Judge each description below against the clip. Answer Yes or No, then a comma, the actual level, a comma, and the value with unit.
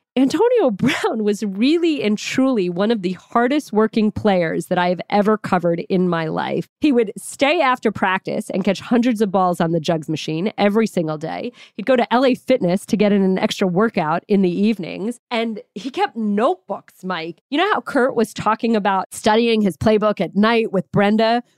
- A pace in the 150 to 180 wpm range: No, average, 195 wpm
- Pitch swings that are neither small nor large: Yes, average, 4.0 semitones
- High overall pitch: Yes, high, 210 Hz